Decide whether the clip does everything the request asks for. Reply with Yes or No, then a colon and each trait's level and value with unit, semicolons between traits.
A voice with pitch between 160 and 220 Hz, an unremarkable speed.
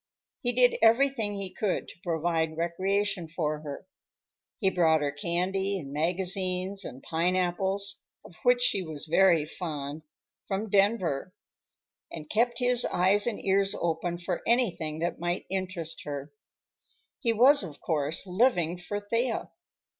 No: medium, 185 Hz; slow, 130 wpm